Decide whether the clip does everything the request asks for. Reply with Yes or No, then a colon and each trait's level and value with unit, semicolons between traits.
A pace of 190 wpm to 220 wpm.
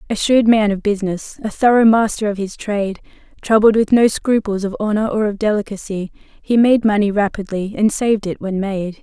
Yes: average, 195 wpm